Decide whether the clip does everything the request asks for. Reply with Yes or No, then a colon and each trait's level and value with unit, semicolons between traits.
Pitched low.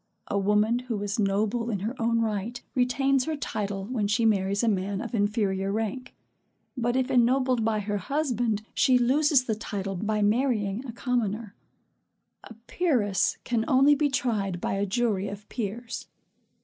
No: high, 225 Hz